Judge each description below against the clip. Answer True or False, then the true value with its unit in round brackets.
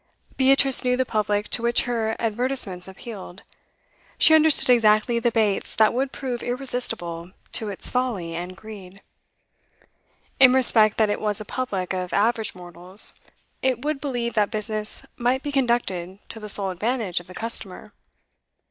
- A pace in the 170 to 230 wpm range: False (155 wpm)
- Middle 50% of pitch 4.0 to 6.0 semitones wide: True (4.3 semitones)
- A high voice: True (220 Hz)